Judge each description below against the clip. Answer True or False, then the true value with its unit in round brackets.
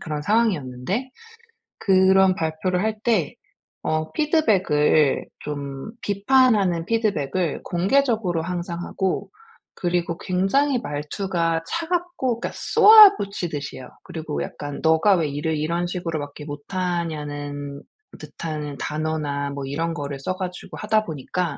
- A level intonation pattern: False (5.2 semitones)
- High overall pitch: False (170 Hz)